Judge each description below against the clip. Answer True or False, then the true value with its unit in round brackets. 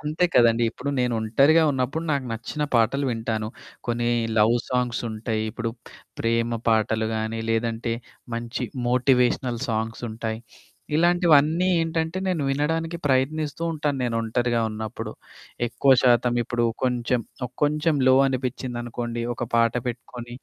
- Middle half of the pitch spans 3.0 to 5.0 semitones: True (3.7 semitones)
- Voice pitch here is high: False (120 Hz)